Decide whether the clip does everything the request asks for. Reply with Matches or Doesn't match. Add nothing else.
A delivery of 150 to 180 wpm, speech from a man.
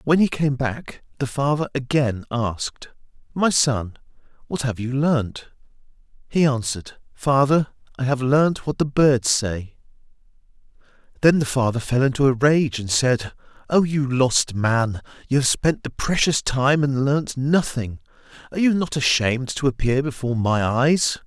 Matches